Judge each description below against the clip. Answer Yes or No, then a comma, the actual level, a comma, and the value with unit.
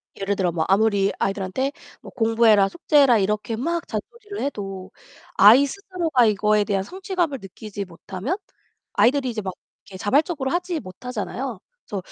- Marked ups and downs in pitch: Yes, wide, 6.4 semitones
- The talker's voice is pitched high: Yes, high, 225 Hz